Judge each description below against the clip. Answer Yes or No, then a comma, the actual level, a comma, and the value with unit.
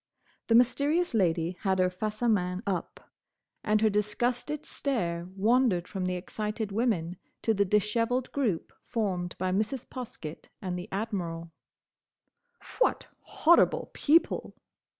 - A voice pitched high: Yes, high, 210 Hz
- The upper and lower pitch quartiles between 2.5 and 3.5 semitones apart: No, average, 4.8 semitones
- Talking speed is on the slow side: Yes, slow, 130 wpm